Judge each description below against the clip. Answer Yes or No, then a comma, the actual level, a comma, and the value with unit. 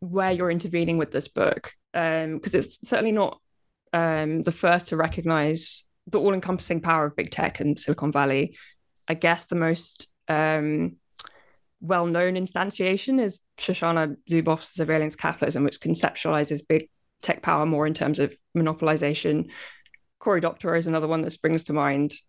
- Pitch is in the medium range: Yes, medium, 165 Hz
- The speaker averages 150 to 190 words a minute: Yes, average, 155 wpm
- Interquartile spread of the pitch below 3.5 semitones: Yes, average, 2.8 semitones